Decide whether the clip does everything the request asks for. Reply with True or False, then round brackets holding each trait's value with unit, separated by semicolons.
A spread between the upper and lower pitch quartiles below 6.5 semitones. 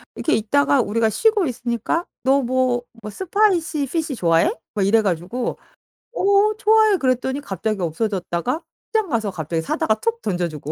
False (9.0 semitones)